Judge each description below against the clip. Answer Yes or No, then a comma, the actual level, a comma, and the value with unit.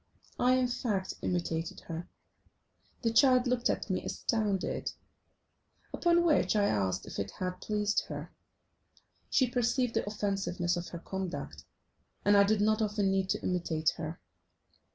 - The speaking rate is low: No, average, 145 wpm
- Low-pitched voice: No, high, 205 Hz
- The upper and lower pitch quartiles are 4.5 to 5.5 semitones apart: Yes, average, 4.9 semitones